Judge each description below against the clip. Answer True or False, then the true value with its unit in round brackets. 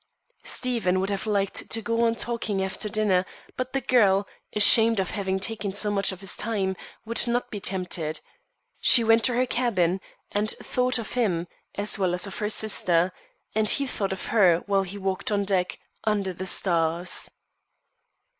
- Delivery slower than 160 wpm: False (180 wpm)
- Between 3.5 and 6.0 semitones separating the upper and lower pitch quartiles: False (3.1 semitones)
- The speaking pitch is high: True (200 Hz)